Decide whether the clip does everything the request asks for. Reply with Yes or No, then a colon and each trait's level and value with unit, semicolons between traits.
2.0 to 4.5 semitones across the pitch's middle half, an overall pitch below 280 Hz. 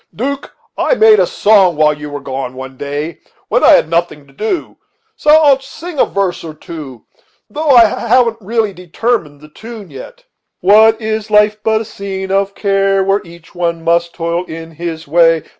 No: average, 5.3 semitones; high, 190 Hz